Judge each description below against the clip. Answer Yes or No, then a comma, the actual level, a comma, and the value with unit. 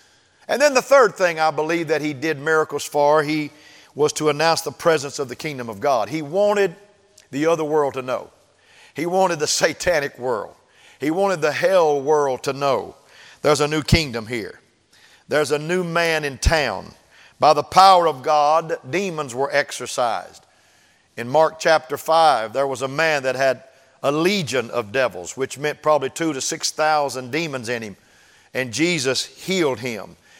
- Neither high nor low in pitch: Yes, medium, 155 Hz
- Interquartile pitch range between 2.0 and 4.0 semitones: Yes, average, 3.1 semitones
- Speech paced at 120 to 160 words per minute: No, average, 175 wpm